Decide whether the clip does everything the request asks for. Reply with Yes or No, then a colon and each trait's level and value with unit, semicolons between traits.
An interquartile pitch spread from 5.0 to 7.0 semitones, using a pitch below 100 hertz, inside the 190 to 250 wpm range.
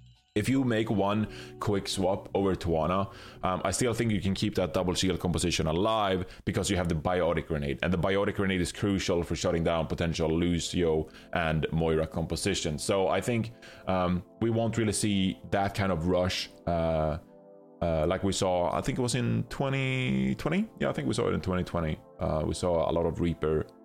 No: average, 3.3 semitones; very low, 90 Hz; average, 195 wpm